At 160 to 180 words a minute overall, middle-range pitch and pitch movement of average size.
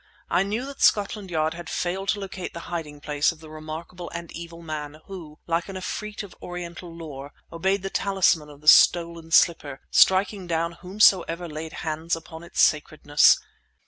Yes: average, 175 wpm; medium, 170 Hz; average, 3.1 semitones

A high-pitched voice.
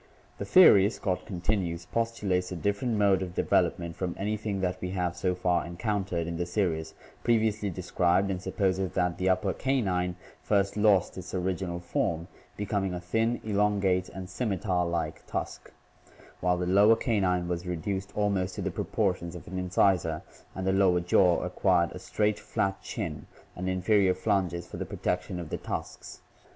No: very low, 95 Hz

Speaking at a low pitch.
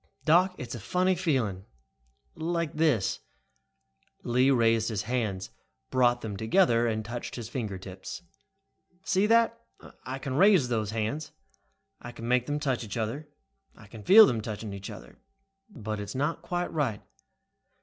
Yes: low, 120 Hz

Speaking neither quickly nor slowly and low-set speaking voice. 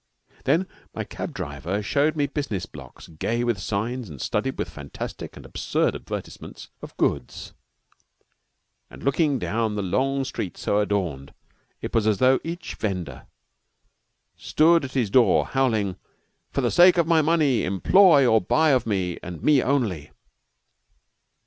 Yes: average, 150 wpm; low, 120 Hz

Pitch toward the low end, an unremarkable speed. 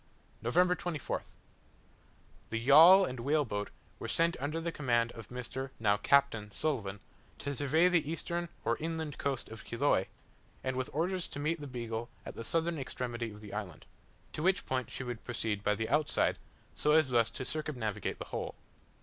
Yes: low, 130 Hz; average, 175 wpm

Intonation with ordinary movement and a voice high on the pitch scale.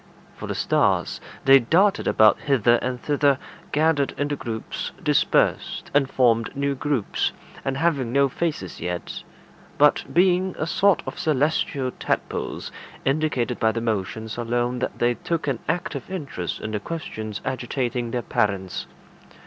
No: average, 4.3 semitones; low, 130 Hz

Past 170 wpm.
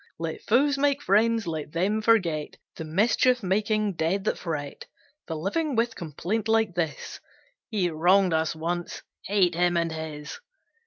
No: average, 150 wpm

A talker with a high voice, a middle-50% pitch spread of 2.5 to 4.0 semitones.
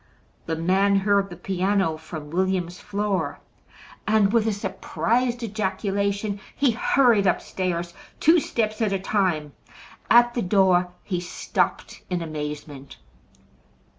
Yes: high, 195 Hz; average, 3.4 semitones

